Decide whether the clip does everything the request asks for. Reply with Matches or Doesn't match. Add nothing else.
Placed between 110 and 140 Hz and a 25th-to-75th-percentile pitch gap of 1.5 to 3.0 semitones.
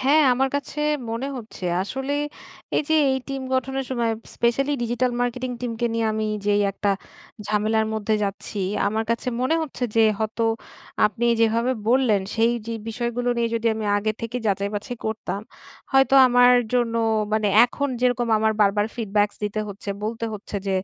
Doesn't match